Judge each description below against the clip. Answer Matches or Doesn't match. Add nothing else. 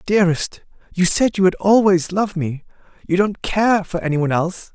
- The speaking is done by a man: Matches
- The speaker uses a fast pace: Doesn't match